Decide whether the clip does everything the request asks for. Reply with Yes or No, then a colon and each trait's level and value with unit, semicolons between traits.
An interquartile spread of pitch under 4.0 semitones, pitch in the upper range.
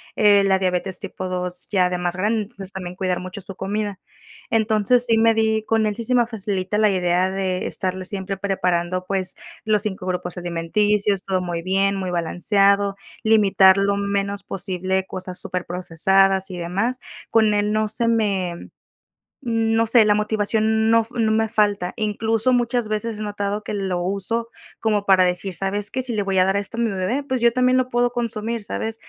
Yes: average, 2.9 semitones; high, 200 Hz